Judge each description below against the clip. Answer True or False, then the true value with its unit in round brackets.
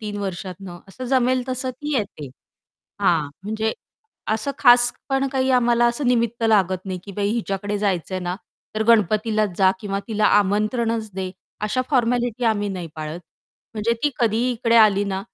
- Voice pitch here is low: False (215 Hz)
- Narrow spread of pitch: False (3.6 semitones)